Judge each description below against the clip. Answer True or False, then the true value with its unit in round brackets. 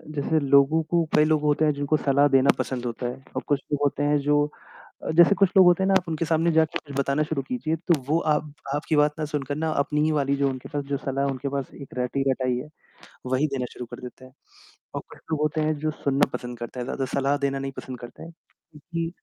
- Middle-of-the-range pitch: True (145 Hz)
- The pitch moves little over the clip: True (2.3 semitones)